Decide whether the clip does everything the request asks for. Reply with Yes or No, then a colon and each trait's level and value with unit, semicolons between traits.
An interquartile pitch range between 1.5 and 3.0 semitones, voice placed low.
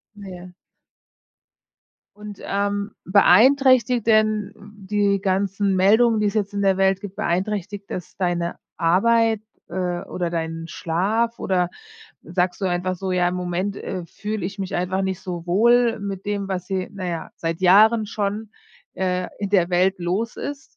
No: narrow, 2.5 semitones; high, 195 Hz